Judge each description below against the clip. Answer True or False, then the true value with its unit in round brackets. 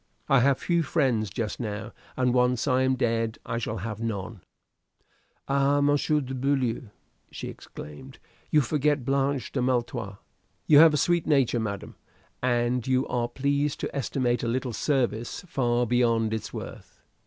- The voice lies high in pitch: False (125 Hz)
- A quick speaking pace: False (155 wpm)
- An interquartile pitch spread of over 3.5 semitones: False (3.2 semitones)